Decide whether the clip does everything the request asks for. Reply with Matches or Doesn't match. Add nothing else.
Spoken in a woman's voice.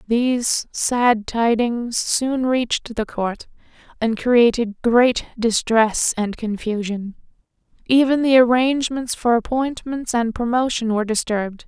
Matches